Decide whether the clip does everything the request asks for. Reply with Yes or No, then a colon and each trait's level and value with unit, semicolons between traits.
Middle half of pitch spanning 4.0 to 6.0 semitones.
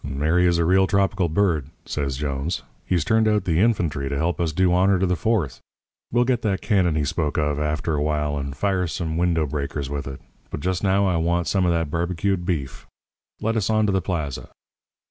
Yes: average, 4.3 semitones